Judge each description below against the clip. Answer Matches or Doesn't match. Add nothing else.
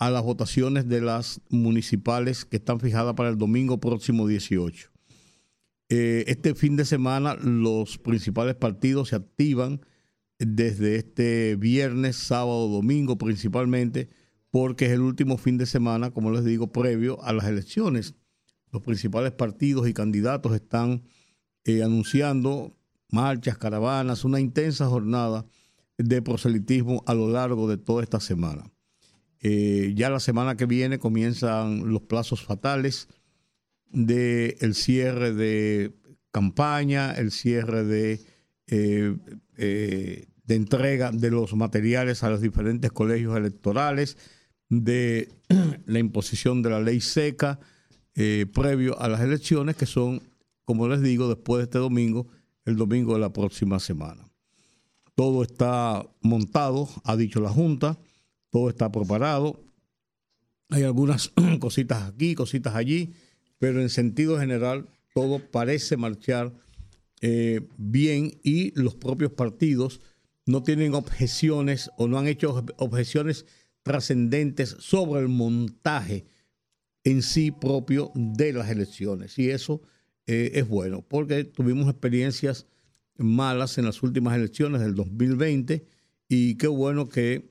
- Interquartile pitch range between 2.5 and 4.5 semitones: Matches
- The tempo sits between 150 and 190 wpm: Doesn't match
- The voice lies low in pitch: Matches